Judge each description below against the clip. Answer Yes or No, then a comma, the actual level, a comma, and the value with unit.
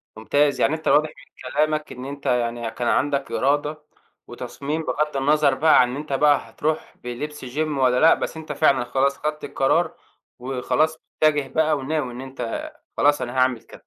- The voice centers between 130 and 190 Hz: Yes, medium, 140 Hz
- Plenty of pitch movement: No, average, 3.1 semitones